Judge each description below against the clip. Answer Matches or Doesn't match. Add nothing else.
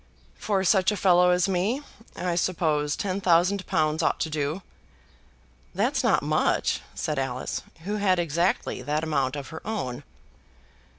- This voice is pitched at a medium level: Matches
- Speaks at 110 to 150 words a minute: Matches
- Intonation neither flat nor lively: Matches